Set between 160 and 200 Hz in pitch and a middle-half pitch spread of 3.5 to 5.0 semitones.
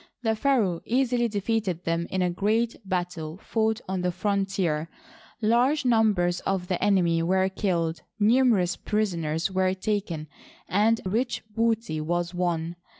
Yes: high, 190 Hz; average, 4.2 semitones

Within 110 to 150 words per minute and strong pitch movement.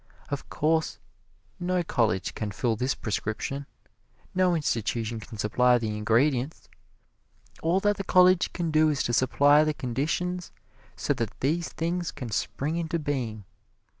Yes: average, 140 wpm; wide, 6.3 semitones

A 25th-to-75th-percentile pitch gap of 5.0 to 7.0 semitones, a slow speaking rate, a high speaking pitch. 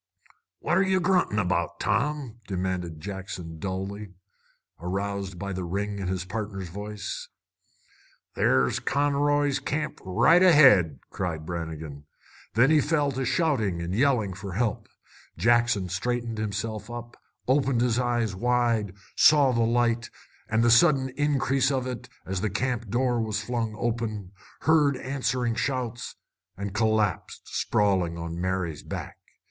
No: average, 5.3 semitones; slow, 130 wpm; low, 110 Hz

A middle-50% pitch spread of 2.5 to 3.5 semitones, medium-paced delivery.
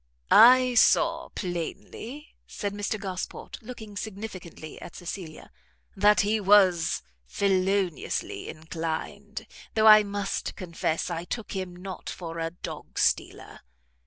No: average, 3.2 semitones; slow, 115 wpm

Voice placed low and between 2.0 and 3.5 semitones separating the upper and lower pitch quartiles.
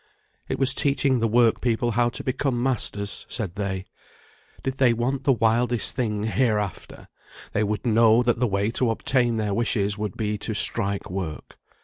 Yes: low, 115 Hz; average, 2.9 semitones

